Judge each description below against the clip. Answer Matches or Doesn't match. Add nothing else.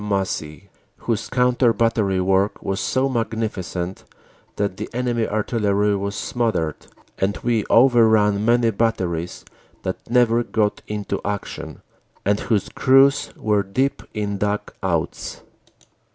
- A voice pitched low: Matches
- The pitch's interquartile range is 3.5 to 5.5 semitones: Doesn't match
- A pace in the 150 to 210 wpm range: Doesn't match